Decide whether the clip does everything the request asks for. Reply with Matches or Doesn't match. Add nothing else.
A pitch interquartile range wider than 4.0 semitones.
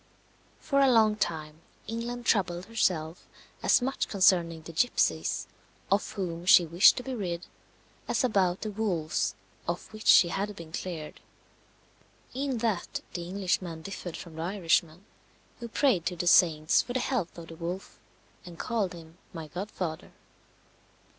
Matches